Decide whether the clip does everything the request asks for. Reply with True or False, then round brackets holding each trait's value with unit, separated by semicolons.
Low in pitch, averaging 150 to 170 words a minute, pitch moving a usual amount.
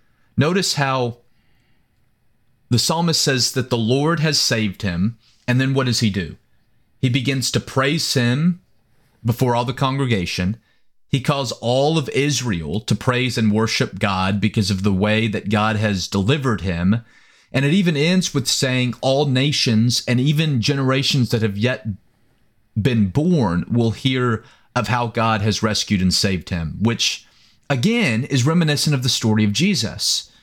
True (120 Hz; 160 wpm; 3.8 semitones)